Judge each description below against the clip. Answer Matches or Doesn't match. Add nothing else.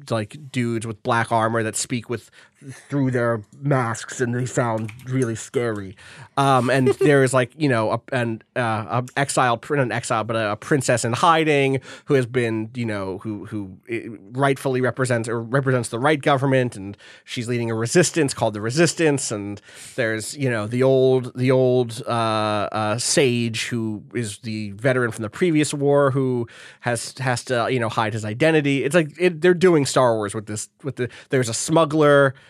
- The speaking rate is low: Doesn't match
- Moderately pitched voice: Doesn't match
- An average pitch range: Matches